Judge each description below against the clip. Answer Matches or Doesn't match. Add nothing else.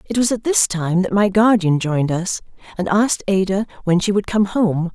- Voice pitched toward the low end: Doesn't match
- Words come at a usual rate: Doesn't match